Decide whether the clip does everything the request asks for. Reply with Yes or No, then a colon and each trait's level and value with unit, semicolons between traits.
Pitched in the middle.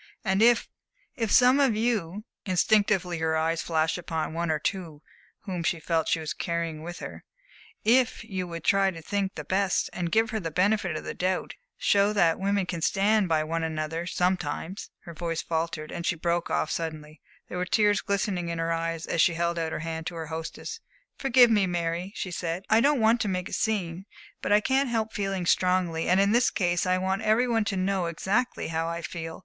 Yes: medium, 180 Hz